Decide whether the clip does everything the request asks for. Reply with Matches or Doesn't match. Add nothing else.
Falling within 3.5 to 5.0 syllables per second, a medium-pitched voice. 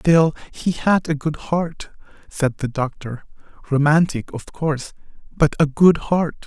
Matches